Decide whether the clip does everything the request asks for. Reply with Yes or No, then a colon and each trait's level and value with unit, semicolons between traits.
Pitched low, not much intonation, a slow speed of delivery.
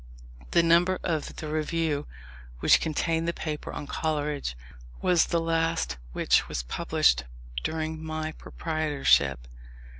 No: medium, 155 Hz; narrow, 2.0 semitones; slow, 120 wpm